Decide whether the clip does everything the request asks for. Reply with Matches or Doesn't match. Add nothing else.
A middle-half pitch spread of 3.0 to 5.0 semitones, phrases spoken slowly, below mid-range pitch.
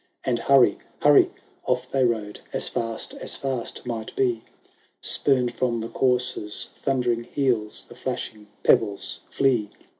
Doesn't match